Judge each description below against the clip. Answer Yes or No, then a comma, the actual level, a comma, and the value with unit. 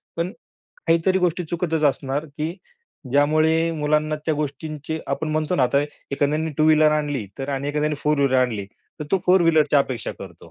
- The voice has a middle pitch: Yes, medium, 150 Hz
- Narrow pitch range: Yes, narrow, 2.2 semitones